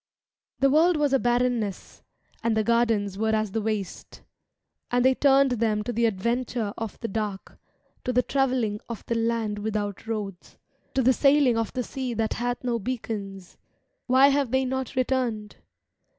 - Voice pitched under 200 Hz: No, high, 235 Hz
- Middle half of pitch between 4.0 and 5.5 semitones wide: No, average, 3.2 semitones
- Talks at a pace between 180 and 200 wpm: No, average, 165 wpm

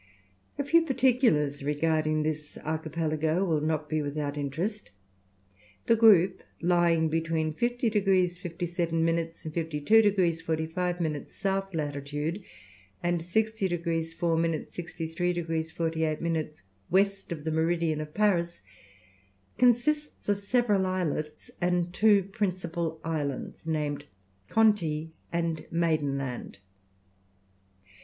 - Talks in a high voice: No, medium, 165 Hz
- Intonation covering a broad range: No, average, 3.2 semitones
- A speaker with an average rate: No, slow, 115 wpm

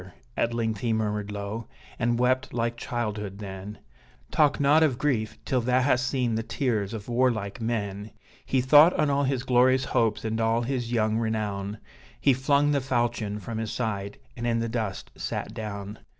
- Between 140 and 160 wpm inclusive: No, average, 180 wpm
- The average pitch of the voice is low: Yes, low, 115 Hz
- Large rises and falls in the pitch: No, average, 3.1 semitones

